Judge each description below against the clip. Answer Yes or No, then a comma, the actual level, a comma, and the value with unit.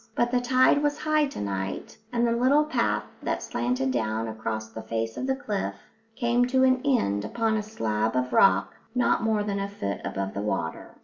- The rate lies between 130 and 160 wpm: No, average, 200 wpm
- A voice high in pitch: Yes, high, 200 Hz